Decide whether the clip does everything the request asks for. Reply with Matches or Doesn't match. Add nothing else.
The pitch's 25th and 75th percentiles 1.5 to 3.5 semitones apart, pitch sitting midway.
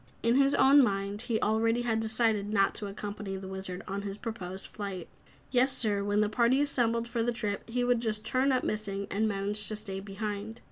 Doesn't match